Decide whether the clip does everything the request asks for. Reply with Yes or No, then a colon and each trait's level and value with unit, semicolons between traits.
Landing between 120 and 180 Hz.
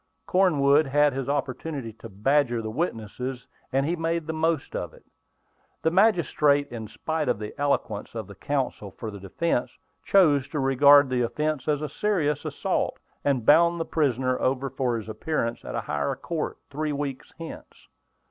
Yes: medium, 140 Hz